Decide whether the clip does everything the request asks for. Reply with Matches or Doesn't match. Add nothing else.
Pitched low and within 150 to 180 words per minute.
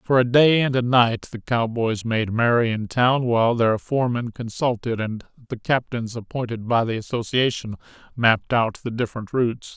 Matches